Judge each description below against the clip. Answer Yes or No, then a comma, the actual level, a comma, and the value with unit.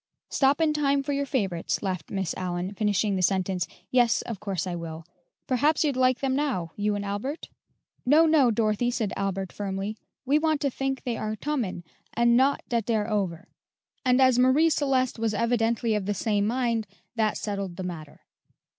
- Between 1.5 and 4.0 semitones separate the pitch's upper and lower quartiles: No, average, 5.0 semitones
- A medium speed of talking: Yes, average, 180 wpm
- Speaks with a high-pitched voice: Yes, high, 225 Hz